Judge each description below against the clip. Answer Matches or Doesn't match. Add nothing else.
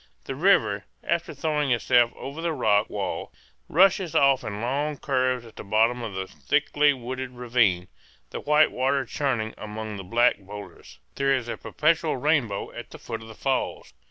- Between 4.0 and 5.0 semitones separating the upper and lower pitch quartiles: Matches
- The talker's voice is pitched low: Matches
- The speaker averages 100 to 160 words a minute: Doesn't match